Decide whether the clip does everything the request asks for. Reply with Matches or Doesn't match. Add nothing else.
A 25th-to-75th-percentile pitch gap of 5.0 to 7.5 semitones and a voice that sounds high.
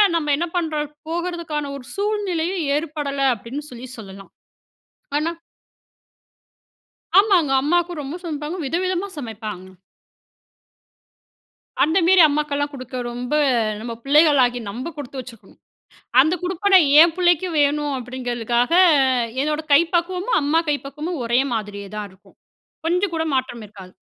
Matches